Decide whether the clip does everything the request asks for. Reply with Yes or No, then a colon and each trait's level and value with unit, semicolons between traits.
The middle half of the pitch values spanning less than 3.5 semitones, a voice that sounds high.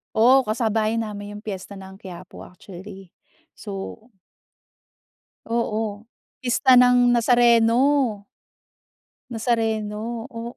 Yes: narrow, 2.6 semitones; high, 225 Hz